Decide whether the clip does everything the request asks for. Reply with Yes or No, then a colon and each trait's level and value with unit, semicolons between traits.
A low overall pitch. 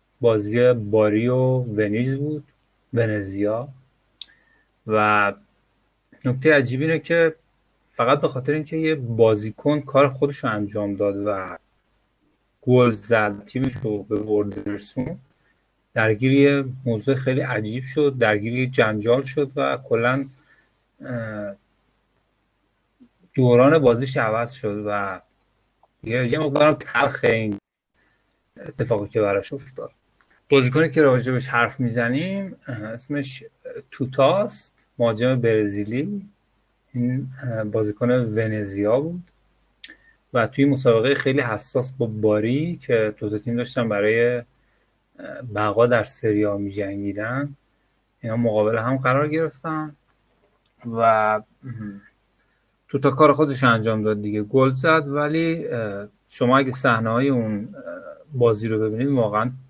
Yes: low, 120 Hz